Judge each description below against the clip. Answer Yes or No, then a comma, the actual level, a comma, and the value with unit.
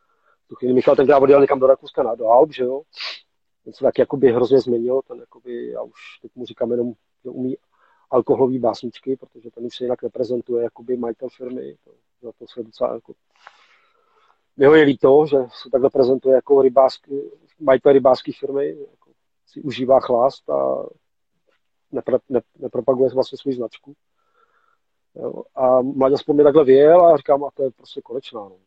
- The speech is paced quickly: Yes, fast, 170 wpm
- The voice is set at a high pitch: No, low, 135 Hz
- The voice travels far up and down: No, narrow, 2.4 semitones